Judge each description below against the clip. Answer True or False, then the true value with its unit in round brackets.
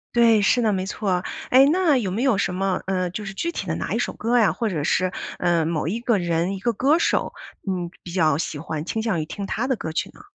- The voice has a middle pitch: False (195 Hz)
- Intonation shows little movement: False (5.0 semitones)